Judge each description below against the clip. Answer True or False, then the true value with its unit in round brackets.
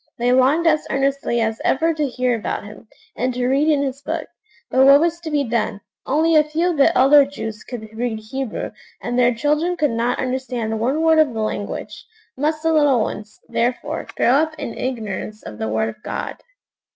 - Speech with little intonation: False (4.7 semitones)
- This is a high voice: True (260 Hz)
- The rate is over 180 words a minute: True (200 wpm)